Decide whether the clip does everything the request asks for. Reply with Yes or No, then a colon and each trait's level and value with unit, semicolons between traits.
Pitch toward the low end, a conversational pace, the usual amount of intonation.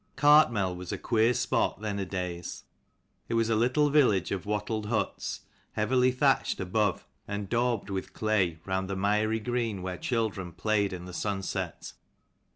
Yes: low, 105 Hz; average, 165 wpm; average, 3.4 semitones